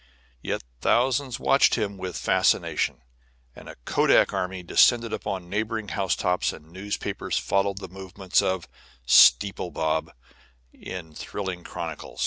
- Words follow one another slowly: Yes, slow, 120 wpm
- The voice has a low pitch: Yes, very low, 95 Hz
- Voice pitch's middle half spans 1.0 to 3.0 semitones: Yes, narrow, 2.4 semitones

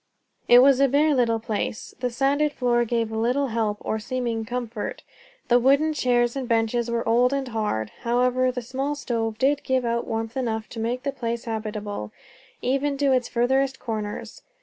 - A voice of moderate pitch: No, high, 240 Hz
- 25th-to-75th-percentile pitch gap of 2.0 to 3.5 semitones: Yes, average, 2.7 semitones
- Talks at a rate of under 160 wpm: No, average, 180 wpm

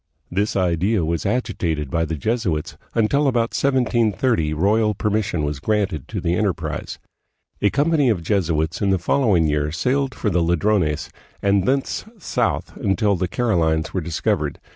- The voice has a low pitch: Yes, very low, 95 Hz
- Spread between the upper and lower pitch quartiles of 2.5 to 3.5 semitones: No, wide, 5.5 semitones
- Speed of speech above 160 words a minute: No, average, 155 wpm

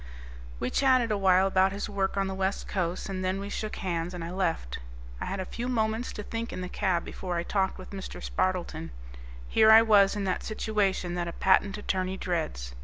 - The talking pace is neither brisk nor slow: No, fast, 215 wpm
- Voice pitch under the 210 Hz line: Yes, high, 190 Hz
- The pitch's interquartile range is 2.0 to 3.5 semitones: Yes, narrow, 2.4 semitones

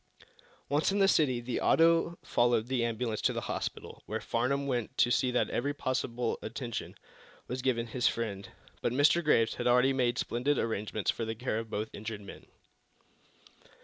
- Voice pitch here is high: No, low, 120 Hz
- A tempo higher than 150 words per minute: Yes, average, 175 wpm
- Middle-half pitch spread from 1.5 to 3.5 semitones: Yes, average, 2.7 semitones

